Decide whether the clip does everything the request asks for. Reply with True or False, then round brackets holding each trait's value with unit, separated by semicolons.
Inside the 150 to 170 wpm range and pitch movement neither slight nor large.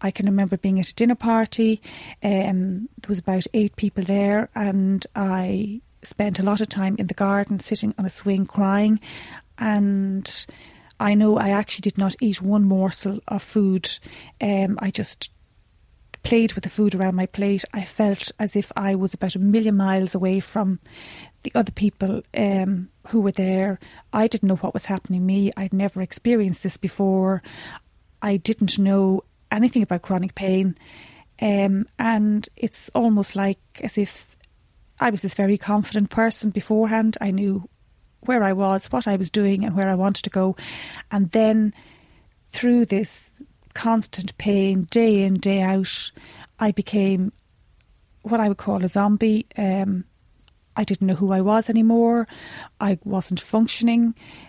False (165 wpm; 1.9 semitones)